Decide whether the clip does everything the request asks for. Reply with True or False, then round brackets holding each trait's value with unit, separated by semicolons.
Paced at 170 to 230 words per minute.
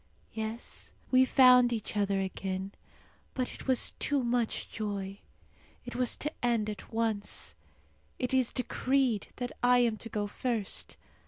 False (145 wpm)